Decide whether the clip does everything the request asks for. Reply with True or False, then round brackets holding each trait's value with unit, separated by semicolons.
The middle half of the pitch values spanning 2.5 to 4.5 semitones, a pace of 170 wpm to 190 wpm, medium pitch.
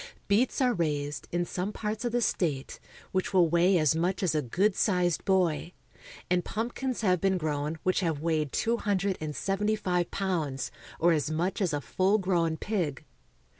True (3.8 semitones; 185 wpm; 180 Hz)